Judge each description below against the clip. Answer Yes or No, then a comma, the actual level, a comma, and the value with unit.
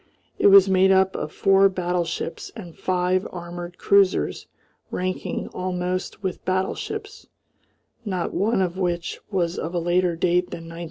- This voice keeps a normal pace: Yes, average, 145 wpm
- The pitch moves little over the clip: Yes, narrow, 1.5 semitones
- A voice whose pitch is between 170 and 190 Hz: Yes, medium, 185 Hz